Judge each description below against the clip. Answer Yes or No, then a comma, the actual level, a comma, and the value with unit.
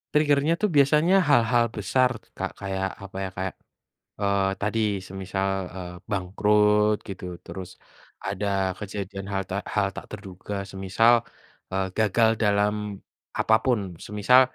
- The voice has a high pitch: No, low, 100 Hz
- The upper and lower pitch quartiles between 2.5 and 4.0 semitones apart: Yes, average, 2.8 semitones